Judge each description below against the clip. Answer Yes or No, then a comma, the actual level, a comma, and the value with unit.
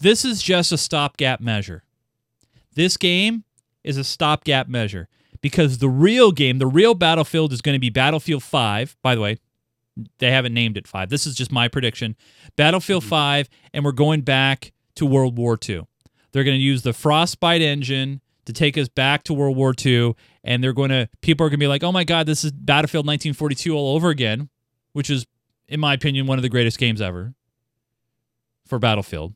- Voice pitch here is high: No, low, 135 Hz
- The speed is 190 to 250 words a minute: Yes, average, 195 wpm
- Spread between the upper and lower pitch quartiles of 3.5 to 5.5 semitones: Yes, average, 4.2 semitones